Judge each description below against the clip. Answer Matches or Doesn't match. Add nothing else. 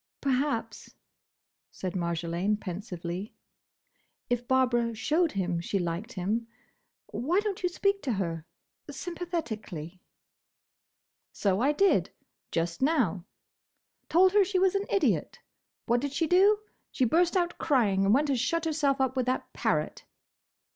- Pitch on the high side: Matches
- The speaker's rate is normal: Doesn't match